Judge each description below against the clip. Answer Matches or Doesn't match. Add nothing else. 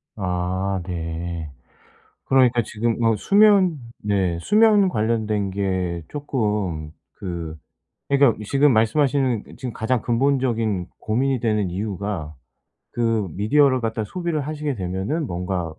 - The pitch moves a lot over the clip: Matches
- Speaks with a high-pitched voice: Doesn't match